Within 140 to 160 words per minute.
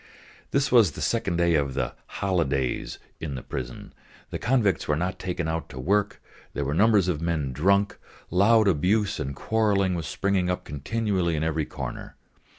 No: average, 170 wpm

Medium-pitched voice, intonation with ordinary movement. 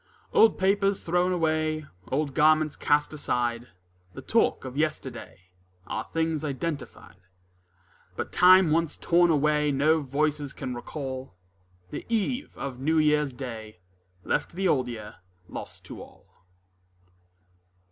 Yes: medium, 150 Hz; average, 3.8 semitones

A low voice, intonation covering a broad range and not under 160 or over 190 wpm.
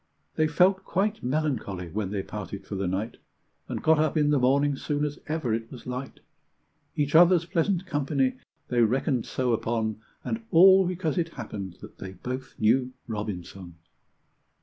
Yes: low, 130 Hz; wide, 6.4 semitones; average, 165 wpm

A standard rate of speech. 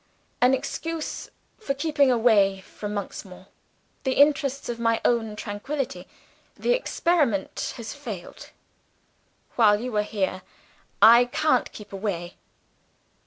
No: slow, 120 wpm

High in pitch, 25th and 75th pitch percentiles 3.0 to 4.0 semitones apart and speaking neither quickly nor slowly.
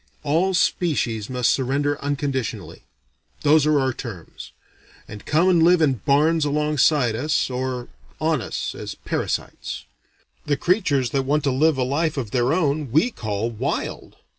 No: medium, 140 Hz; average, 3.5 semitones; average, 150 wpm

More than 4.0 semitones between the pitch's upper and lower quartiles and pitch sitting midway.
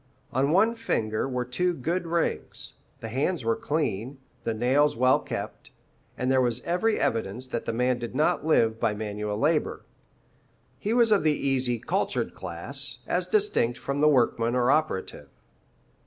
No: average, 5.3 semitones; low, 130 Hz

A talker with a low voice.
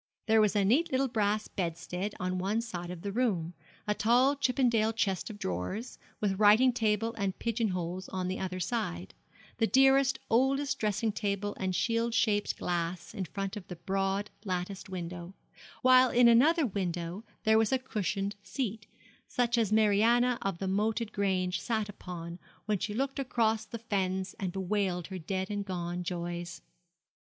No: high, 205 Hz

